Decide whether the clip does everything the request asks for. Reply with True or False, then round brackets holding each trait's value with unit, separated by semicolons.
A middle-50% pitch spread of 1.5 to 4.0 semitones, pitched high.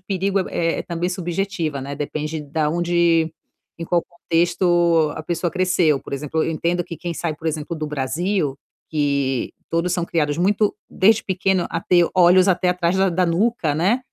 False (2.7 semitones; 170 Hz)